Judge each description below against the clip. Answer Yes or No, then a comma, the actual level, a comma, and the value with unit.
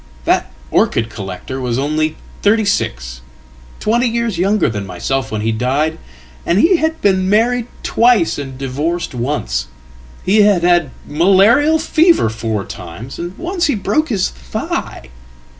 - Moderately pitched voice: Yes, medium, 170 Hz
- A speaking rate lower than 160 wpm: Yes, slow, 135 wpm